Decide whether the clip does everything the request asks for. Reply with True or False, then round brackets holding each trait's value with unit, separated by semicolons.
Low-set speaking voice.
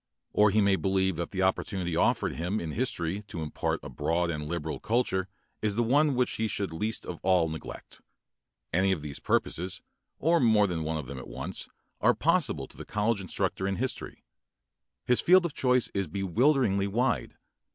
True (95 Hz)